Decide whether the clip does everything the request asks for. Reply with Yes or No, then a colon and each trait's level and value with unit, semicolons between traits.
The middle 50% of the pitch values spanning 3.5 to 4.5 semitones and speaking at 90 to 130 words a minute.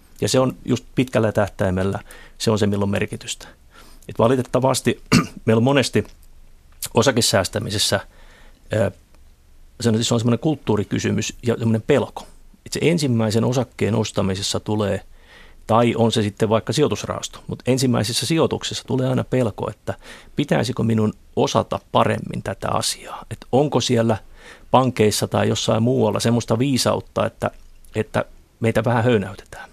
No: average, 2.8 semitones; average, 125 wpm